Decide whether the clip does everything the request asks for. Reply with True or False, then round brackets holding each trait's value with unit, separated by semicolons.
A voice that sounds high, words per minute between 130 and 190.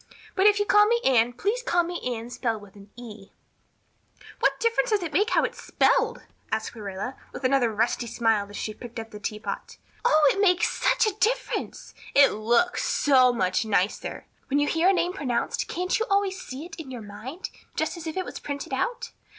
False (280 Hz; 205 wpm)